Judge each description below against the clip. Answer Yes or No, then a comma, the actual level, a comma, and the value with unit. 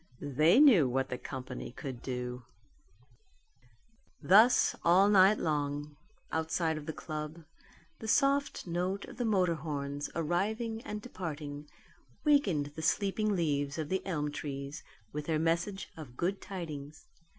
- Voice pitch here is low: No, medium, 160 Hz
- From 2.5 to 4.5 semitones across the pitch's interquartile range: No, average, 5.0 semitones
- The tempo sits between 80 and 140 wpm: Yes, slow, 135 wpm